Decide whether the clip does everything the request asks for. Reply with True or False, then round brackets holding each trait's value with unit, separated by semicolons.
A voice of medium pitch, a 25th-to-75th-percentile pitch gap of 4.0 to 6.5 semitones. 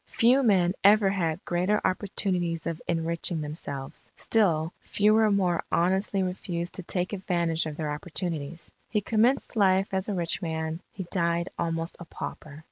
False (175 Hz; 3.0 semitones)